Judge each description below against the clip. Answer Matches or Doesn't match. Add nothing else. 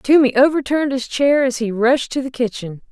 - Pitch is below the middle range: Doesn't match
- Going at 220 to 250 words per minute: Doesn't match